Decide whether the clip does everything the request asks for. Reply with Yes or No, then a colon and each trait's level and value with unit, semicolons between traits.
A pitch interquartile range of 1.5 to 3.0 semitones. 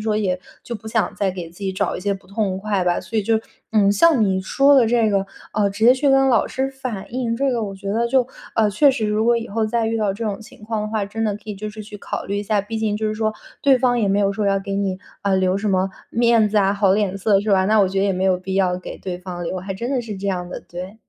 Yes: average, 2.7 semitones